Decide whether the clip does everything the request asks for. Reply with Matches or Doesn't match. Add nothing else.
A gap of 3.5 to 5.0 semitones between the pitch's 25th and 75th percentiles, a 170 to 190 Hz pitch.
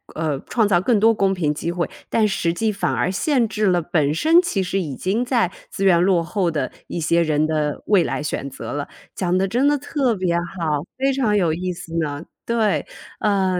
Matches